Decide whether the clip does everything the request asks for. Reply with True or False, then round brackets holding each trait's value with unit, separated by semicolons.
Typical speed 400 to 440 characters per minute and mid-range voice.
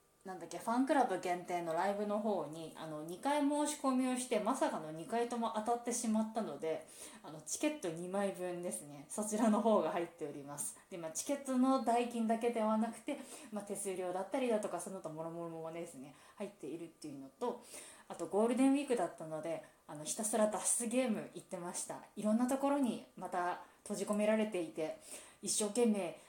False (410 characters per minute; 205 Hz)